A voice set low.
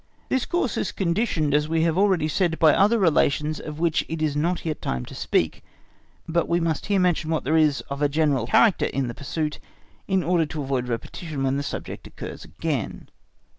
No: medium, 155 Hz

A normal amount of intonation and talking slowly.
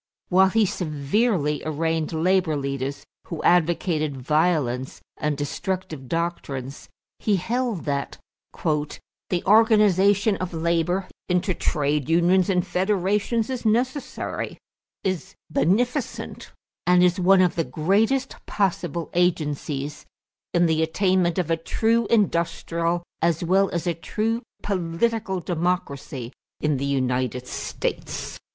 Yes: average, 4.2 semitones; slow, 115 wpm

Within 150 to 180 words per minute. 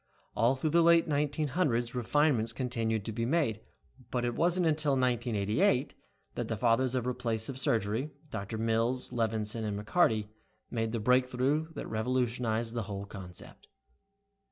No: average, 140 wpm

